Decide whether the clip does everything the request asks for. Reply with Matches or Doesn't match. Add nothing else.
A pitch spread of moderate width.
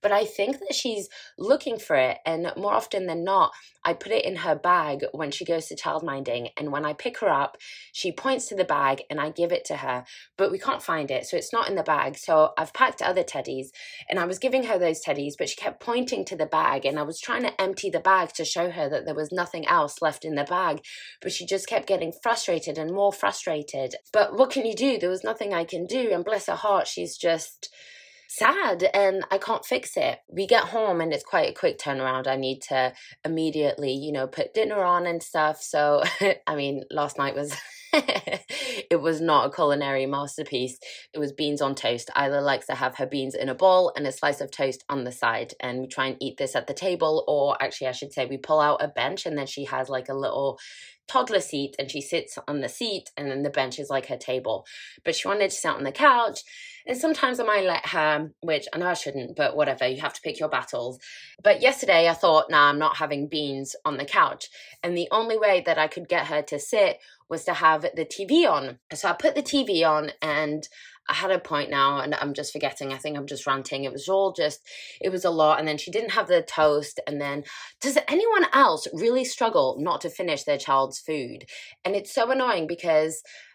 Doesn't match